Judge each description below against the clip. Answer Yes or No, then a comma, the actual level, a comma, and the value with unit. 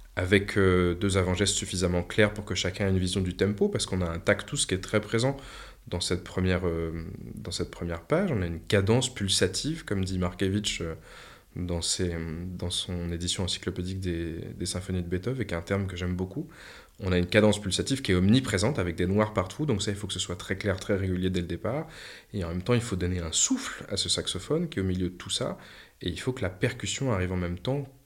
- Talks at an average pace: No, fast, 240 wpm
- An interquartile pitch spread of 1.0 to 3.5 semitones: Yes, average, 3.0 semitones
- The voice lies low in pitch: Yes, very low, 95 Hz